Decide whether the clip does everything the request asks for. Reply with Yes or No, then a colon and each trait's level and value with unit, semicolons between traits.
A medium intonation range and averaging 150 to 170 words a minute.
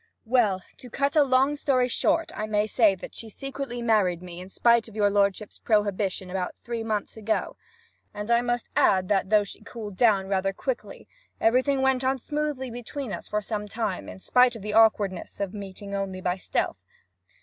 No: average, 3.9 semitones; average, 195 wpm